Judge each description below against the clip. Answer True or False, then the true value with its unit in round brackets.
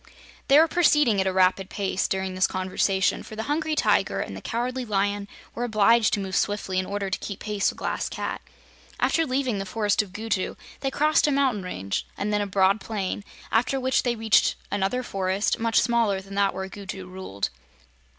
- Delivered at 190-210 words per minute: True (200 wpm)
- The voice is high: True (205 Hz)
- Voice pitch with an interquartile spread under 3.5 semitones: False (3.8 semitones)